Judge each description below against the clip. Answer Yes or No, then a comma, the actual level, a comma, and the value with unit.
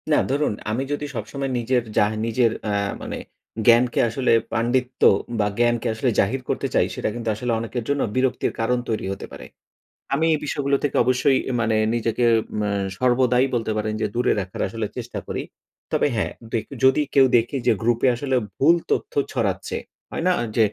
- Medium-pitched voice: No, low, 120 Hz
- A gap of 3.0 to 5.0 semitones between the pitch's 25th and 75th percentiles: No, narrow, 2.6 semitones